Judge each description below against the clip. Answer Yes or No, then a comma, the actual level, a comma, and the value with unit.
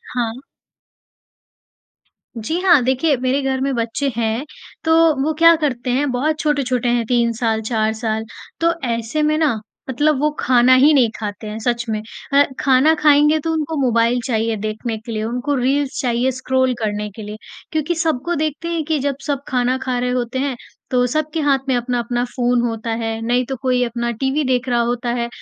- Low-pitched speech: No, very high, 250 Hz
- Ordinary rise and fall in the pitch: Yes, average, 3.4 semitones